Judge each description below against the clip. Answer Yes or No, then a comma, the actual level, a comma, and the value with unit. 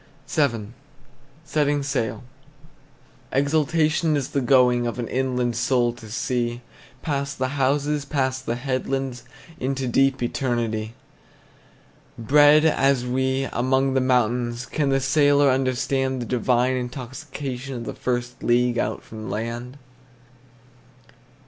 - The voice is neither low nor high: No, low, 130 Hz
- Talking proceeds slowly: Yes, slow, 115 wpm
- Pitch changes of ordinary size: No, narrow, 2.3 semitones